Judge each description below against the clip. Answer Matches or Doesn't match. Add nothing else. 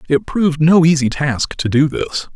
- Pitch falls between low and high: Matches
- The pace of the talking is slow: Doesn't match